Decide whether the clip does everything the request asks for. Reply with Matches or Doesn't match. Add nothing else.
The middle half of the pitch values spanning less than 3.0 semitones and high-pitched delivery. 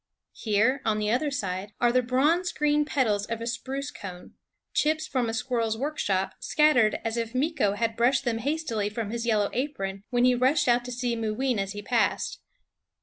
Doesn't match